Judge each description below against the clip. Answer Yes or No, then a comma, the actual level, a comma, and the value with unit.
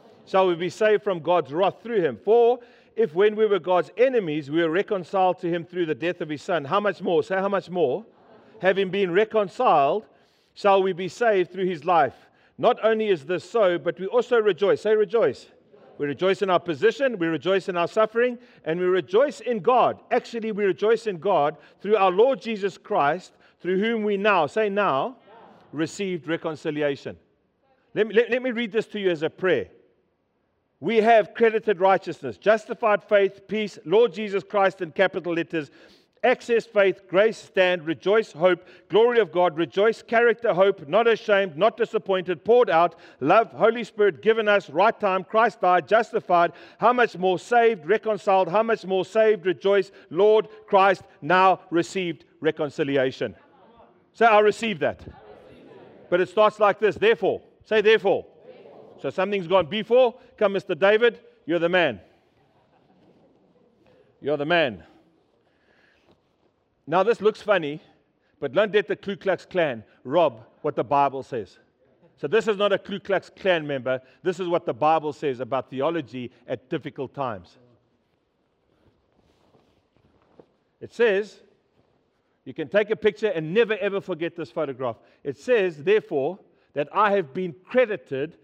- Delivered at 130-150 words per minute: No, average, 160 wpm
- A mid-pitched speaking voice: No, high, 195 Hz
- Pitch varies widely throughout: No, average, 4.3 semitones